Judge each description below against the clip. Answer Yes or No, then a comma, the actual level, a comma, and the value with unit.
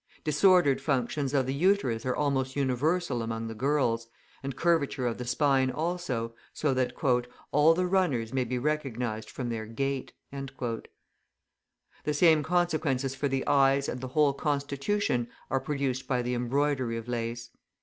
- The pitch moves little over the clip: No, average, 3.3 semitones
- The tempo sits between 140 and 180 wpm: Yes, average, 150 wpm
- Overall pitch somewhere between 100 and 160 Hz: Yes, low, 135 Hz